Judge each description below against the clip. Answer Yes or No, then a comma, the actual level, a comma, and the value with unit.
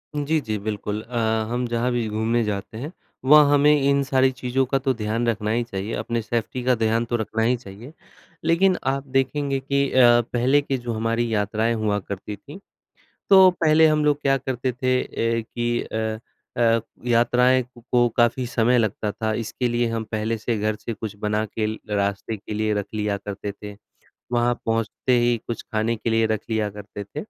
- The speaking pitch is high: No, low, 115 Hz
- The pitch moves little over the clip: No, average, 3.0 semitones